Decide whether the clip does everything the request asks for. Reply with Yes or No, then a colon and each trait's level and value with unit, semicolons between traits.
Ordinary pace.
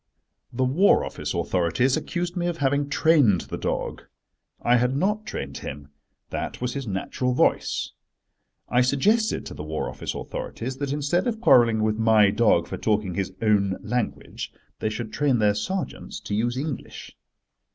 Yes: average, 160 wpm